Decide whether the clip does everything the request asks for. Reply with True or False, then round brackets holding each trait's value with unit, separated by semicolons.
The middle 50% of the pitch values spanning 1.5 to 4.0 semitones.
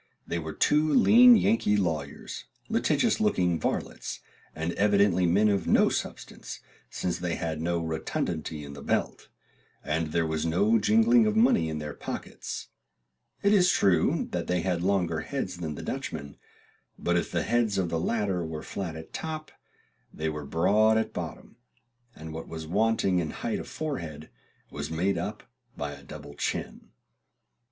False (5.0 semitones)